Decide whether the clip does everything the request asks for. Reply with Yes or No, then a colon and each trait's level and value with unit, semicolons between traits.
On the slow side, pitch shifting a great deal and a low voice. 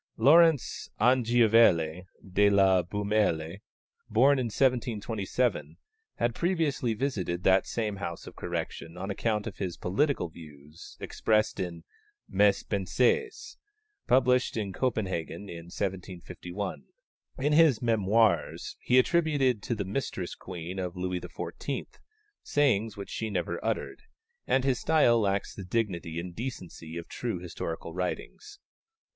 Yes: slow, 125 wpm; wide, 5.8 semitones; low, 105 Hz